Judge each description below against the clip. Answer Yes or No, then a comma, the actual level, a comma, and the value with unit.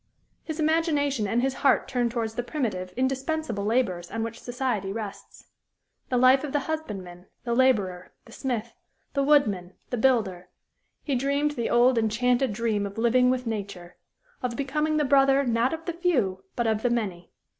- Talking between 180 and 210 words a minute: No, average, 170 wpm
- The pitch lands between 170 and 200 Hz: No, high, 245 Hz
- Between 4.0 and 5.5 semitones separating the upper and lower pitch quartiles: Yes, average, 4.4 semitones